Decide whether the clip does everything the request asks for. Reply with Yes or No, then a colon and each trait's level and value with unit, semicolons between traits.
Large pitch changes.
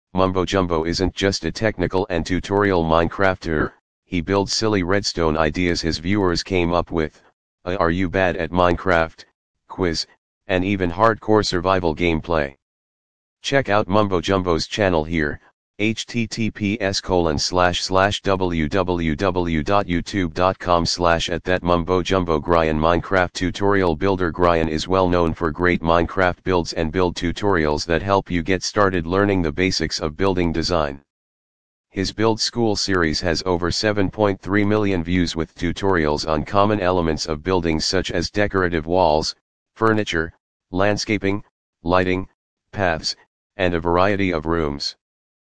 No: average, 2.8 semitones